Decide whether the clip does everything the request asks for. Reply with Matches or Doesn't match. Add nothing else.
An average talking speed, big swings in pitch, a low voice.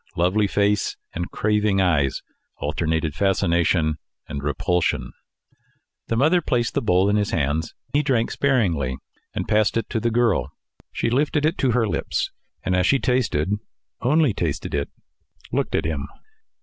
Matches